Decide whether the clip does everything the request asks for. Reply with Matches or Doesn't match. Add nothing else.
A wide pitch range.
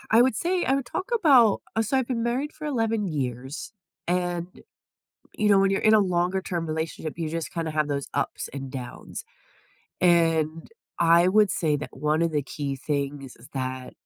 Matches